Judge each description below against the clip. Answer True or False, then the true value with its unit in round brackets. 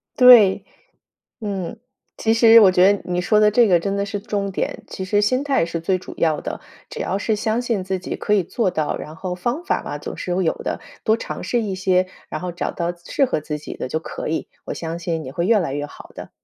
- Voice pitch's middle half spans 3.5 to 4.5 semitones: True (4.0 semitones)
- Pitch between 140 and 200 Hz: True (190 Hz)